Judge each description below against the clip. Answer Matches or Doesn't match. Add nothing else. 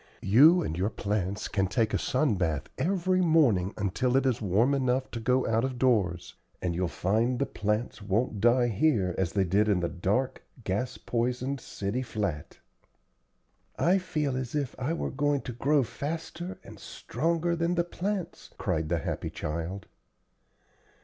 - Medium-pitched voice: Doesn't match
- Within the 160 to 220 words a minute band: Matches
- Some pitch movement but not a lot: Doesn't match